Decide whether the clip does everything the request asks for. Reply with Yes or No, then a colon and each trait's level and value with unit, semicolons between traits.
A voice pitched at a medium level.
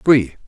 No: low, 125 Hz